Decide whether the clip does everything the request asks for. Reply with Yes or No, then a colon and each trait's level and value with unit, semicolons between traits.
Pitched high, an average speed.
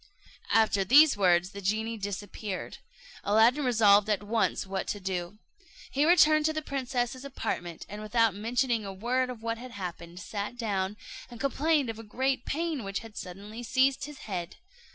Yes: high, 225 Hz; average, 170 wpm